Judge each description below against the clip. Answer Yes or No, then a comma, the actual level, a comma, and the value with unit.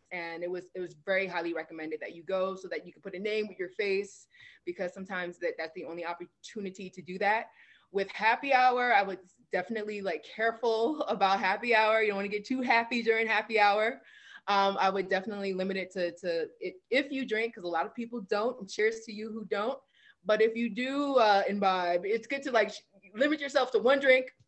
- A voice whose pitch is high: Yes, high, 210 Hz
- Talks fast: Yes, fast, 220 wpm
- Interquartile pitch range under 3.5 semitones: No, average, 3.9 semitones